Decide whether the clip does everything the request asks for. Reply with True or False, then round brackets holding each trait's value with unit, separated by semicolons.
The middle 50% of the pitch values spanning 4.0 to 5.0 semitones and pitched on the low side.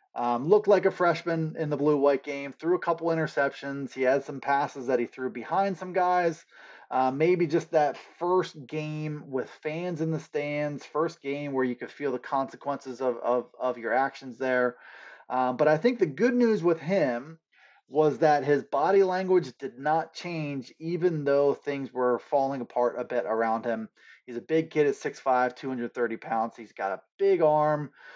False (4.6 semitones; 145 Hz)